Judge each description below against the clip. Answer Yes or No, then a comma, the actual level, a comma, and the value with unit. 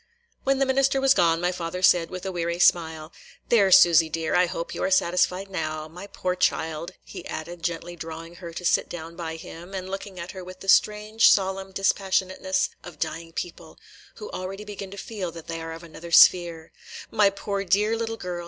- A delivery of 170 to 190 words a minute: No, fast, 205 wpm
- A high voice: No, medium, 180 Hz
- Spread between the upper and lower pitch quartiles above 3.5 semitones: No, average, 2.7 semitones